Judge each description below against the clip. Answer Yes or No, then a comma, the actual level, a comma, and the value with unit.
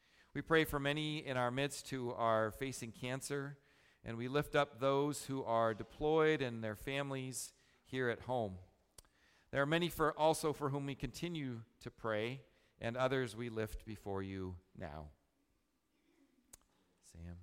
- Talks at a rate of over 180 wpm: No, average, 150 wpm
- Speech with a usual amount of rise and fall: Yes, average, 4.4 semitones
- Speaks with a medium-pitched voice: No, low, 130 Hz